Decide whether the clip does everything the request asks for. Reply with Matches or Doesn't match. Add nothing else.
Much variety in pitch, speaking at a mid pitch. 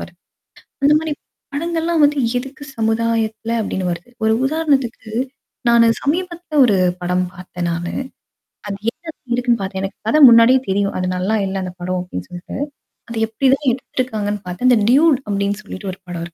Doesn't match